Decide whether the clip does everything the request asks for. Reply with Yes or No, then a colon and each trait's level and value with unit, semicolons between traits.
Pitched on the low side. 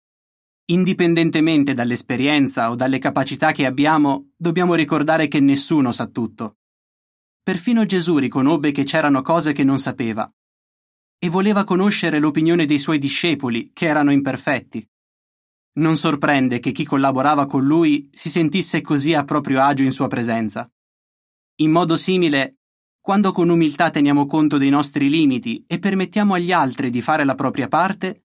No: medium, 155 Hz